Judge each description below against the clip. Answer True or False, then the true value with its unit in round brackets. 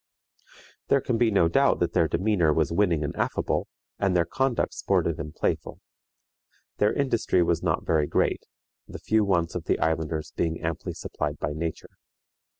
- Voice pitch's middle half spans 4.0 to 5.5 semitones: True (4.4 semitones)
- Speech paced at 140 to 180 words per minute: True (170 wpm)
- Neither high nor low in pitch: False (85 Hz)